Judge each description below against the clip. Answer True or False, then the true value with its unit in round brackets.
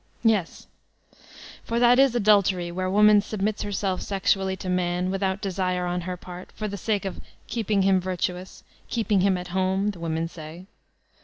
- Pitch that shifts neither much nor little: False (2.3 semitones)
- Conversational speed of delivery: True (165 wpm)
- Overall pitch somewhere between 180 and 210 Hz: True (190 Hz)